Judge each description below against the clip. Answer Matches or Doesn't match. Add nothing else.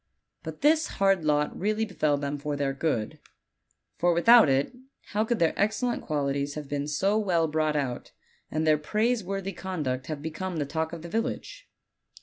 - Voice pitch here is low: Doesn't match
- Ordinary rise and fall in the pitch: Doesn't match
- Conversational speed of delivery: Matches